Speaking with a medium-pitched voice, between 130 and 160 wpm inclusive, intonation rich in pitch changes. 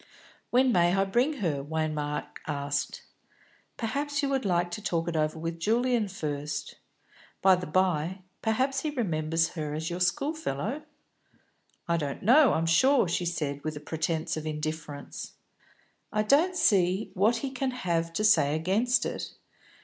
Yes: medium, 175 Hz; average, 155 wpm; wide, 7.1 semitones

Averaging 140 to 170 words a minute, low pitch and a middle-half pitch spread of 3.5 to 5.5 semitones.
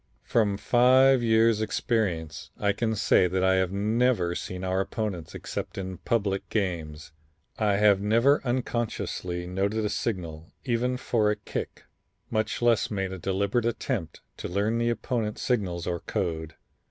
Yes: average, 150 wpm; low, 105 Hz; average, 4.0 semitones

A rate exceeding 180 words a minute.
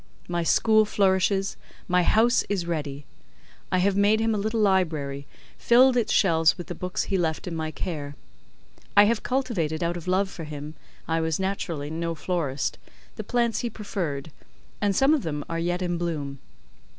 No: average, 175 wpm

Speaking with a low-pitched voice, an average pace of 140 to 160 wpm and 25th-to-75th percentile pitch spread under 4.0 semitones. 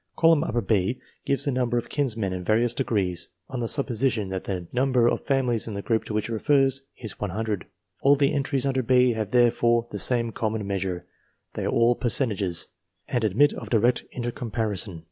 No: low, 115 Hz; average, 190 wpm; average, 3.5 semitones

